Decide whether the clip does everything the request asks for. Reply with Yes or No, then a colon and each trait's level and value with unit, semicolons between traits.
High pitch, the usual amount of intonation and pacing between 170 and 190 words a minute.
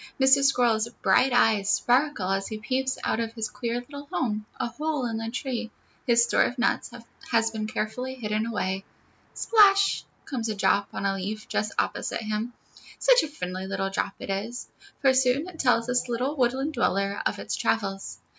Yes: high, 235 Hz; average, 3.6 semitones; average, 185 wpm